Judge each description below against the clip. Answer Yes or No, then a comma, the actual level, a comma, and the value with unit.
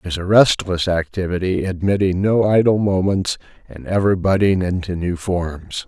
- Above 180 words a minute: No, average, 155 wpm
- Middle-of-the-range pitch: No, very low, 95 Hz